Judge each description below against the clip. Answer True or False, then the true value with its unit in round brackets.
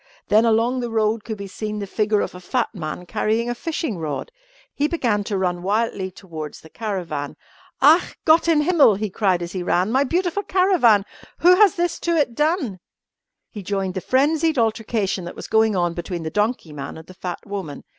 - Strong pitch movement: True (6.3 semitones)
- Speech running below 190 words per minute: False (200 wpm)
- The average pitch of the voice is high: True (215 Hz)